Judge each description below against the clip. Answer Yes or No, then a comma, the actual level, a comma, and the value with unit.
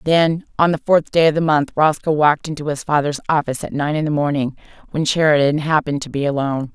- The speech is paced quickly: Yes, fast, 220 wpm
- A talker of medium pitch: Yes, medium, 150 Hz